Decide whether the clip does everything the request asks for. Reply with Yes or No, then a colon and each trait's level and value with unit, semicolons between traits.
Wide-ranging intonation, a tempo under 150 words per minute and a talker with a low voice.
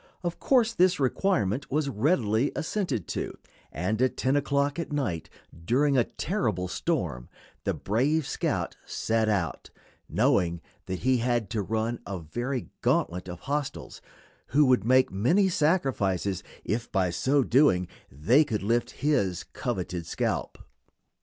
Yes: wide, 6.9 semitones; average, 140 wpm; low, 120 Hz